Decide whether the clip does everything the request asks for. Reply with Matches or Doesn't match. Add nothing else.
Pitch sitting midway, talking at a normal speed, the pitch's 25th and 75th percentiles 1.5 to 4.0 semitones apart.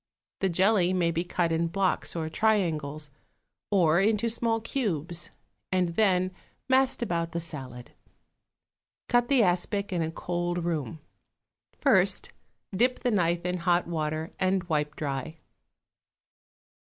Doesn't match